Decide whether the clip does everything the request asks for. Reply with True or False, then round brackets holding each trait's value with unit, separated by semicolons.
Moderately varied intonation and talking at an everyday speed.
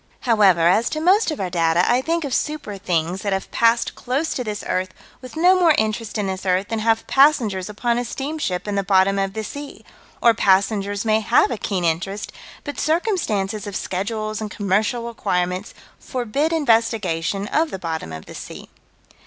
True (4.7 semitones; 185 wpm)